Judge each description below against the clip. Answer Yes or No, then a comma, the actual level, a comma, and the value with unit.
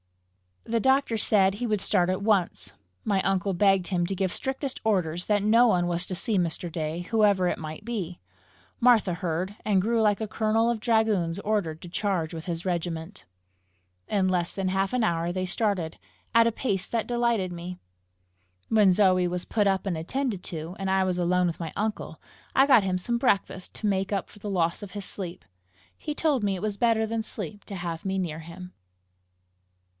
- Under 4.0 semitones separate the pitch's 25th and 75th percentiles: Yes, average, 3.5 semitones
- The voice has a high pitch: Yes, high, 195 Hz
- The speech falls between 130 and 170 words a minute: No, average, 200 wpm